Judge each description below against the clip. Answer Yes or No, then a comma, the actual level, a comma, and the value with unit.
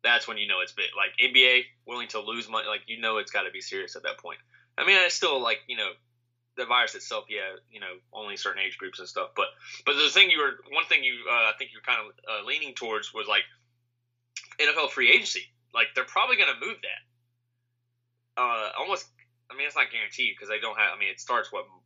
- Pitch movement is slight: Yes, narrow, 1.0 semitones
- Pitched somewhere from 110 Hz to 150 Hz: Yes, low, 120 Hz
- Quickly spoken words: Yes, fast, 240 wpm